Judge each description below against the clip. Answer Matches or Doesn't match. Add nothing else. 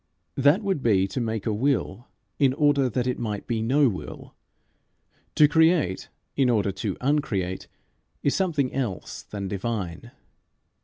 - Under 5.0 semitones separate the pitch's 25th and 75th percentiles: Doesn't match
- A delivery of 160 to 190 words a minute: Doesn't match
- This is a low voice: Matches